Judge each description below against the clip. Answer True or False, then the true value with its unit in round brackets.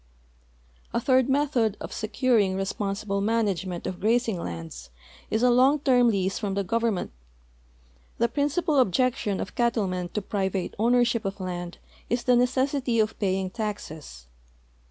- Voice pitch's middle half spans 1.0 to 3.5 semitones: False (4.4 semitones)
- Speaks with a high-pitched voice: True (220 Hz)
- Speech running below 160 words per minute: True (145 wpm)